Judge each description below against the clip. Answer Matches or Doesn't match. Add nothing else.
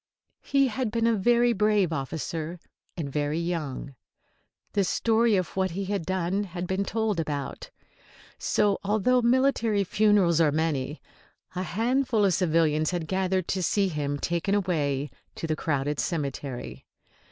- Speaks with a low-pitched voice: Doesn't match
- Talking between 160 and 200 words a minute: Doesn't match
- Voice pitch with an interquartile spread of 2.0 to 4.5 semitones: Doesn't match